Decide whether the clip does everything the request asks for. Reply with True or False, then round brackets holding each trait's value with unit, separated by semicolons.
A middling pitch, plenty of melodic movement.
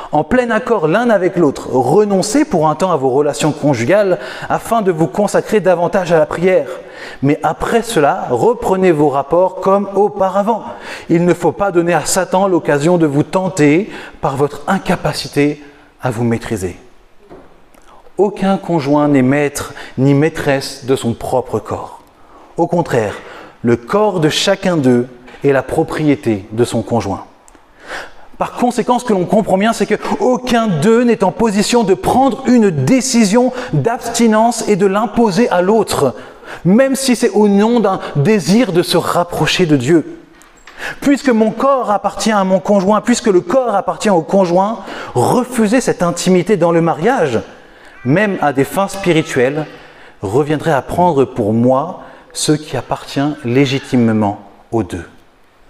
True (180 Hz; 6.6 semitones)